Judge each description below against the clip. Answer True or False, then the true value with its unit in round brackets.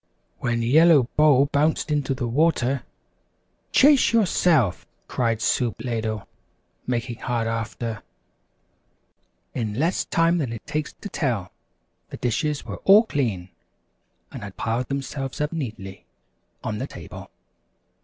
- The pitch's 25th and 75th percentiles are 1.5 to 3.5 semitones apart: False (4.9 semitones)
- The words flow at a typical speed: False (125 wpm)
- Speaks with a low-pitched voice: True (130 Hz)